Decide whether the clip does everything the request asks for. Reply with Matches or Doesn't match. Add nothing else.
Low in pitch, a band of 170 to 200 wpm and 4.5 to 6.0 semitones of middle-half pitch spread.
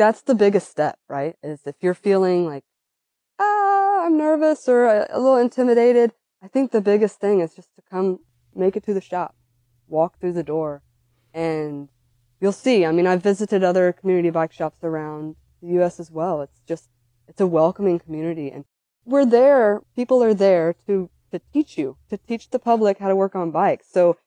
Doesn't match